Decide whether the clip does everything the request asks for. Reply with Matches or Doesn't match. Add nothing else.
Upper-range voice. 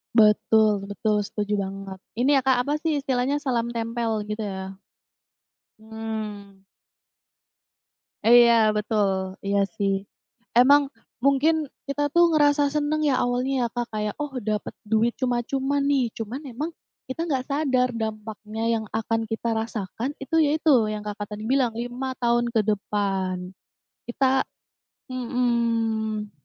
Matches